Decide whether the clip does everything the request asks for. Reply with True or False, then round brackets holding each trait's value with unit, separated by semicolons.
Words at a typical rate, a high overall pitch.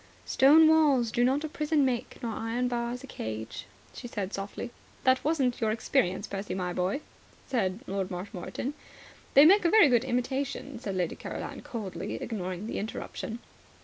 True (165 wpm; 240 Hz)